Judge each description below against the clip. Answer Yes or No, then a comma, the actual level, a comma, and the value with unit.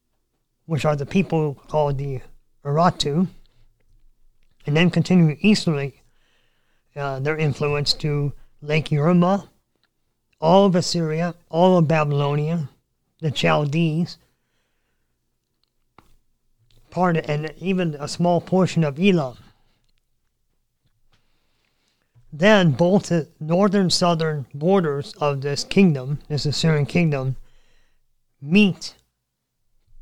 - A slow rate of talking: Yes, slow, 95 wpm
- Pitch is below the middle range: No, medium, 155 Hz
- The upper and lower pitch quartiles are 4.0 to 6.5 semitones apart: No, average, 3.6 semitones